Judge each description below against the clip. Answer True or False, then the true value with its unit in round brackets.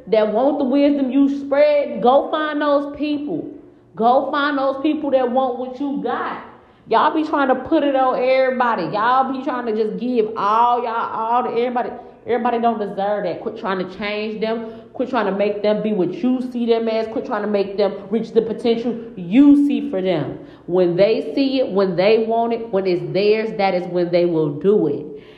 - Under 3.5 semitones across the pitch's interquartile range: False (4.6 semitones)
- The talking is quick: True (210 wpm)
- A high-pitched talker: True (235 Hz)